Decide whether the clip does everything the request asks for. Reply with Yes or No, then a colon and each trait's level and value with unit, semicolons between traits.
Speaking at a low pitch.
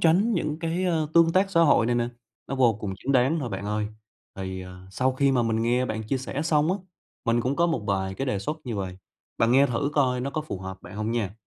Yes: low, 125 Hz